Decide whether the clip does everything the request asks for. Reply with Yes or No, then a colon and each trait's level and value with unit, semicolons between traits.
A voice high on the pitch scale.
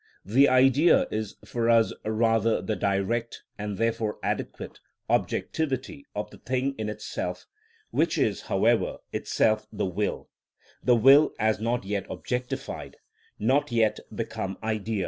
No: low, 115 Hz